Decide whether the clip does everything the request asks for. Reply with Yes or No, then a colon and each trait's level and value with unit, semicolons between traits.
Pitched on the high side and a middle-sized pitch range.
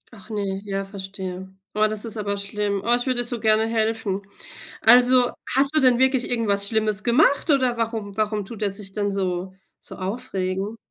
Yes: high, 215 Hz; average, 3.3 semitones